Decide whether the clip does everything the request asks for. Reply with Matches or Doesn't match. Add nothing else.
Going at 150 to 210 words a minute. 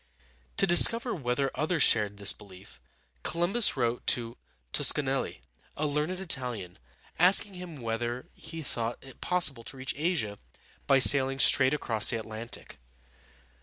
Doesn't match